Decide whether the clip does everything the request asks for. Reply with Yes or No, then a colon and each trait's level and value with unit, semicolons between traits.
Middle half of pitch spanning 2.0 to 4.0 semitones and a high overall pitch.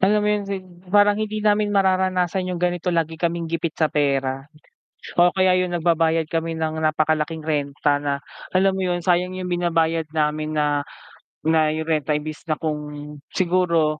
No: average, 3.0 semitones; medium, 165 Hz